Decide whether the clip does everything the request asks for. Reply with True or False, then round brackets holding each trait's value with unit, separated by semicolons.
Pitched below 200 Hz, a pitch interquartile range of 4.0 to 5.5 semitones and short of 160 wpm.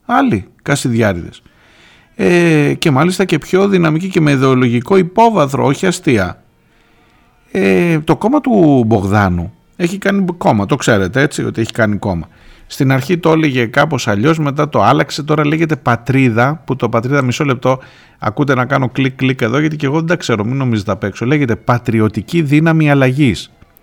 False (140 Hz; 5.2 semitones; 165 wpm)